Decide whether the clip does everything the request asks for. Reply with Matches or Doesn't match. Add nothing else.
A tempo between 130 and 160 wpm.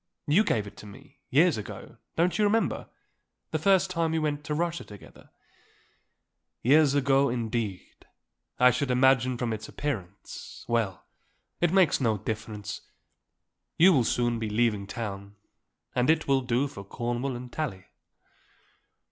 Matches